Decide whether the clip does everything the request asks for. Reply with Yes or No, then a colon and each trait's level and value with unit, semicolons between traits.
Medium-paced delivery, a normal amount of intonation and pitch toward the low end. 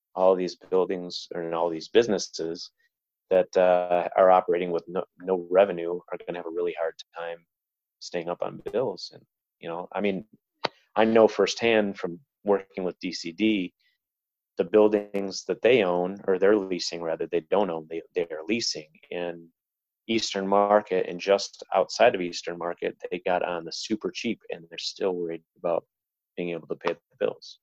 Yes: average, 175 wpm; average, 3.9 semitones; very low, 95 Hz